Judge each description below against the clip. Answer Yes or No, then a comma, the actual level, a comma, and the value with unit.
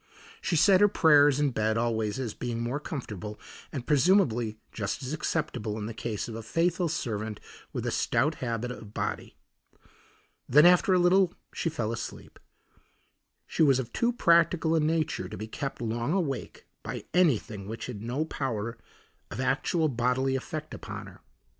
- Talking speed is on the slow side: No, average, 165 wpm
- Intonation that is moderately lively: No, wide, 5.9 semitones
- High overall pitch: No, low, 130 Hz